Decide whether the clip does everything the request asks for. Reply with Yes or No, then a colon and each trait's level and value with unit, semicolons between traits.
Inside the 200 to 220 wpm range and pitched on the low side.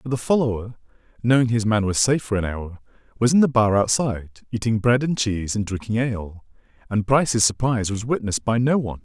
Yes: fast, 205 wpm; low, 115 Hz